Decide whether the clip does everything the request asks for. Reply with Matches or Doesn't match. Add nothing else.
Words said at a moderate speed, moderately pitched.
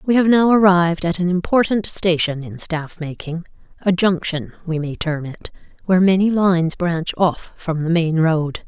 Matches